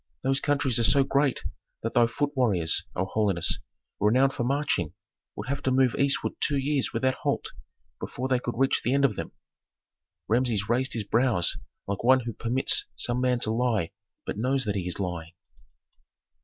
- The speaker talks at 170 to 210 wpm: Yes, average, 180 wpm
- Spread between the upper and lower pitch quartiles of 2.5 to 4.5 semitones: Yes, average, 3.9 semitones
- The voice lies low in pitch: Yes, low, 125 Hz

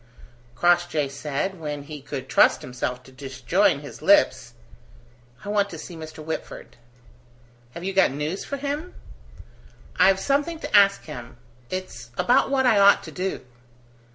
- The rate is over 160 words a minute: No, average, 150 wpm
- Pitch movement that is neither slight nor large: No, wide, 6.0 semitones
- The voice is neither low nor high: Yes, medium, 175 Hz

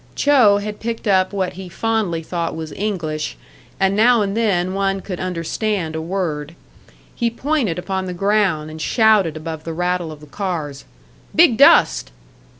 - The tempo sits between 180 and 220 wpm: No, average, 160 wpm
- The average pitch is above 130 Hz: Yes, medium, 185 Hz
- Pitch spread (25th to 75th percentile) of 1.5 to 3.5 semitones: No, average, 4.3 semitones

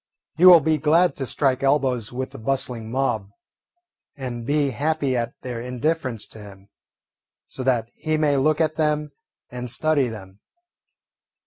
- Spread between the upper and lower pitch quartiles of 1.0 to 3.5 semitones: No, average, 4.1 semitones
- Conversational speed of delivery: Yes, average, 150 wpm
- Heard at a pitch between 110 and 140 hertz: Yes, low, 135 Hz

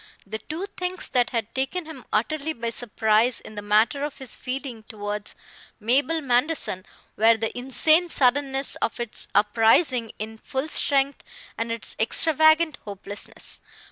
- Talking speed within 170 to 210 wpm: No, average, 140 wpm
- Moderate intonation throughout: Yes, average, 4.8 semitones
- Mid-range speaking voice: No, high, 245 Hz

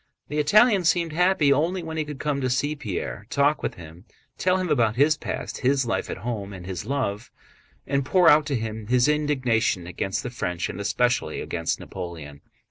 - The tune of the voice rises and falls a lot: Yes, wide, 6.9 semitones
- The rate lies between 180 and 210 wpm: Yes, average, 195 wpm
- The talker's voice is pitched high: No, low, 130 Hz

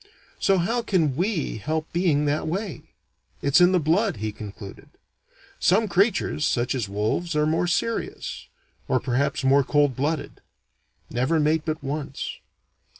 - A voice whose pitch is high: No, medium, 155 Hz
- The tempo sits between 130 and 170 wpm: Yes, average, 145 wpm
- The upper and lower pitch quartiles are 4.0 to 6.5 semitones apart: Yes, average, 4.6 semitones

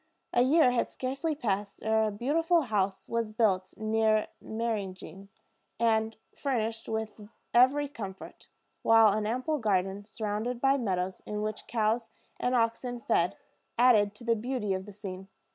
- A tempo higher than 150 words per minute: No, average, 145 wpm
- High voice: Yes, high, 220 Hz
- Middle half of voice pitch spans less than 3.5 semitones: Yes, average, 3.0 semitones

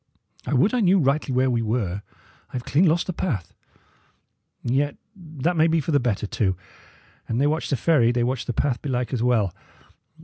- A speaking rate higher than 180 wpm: Yes, average, 200 wpm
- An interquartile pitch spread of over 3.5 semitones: Yes, average, 4.9 semitones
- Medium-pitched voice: No, low, 130 Hz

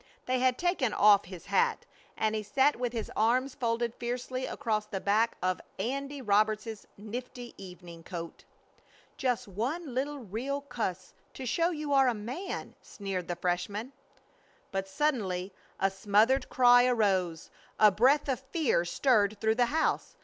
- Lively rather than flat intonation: No, average, 4.6 semitones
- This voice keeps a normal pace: Yes, average, 150 wpm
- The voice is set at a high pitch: Yes, high, 230 Hz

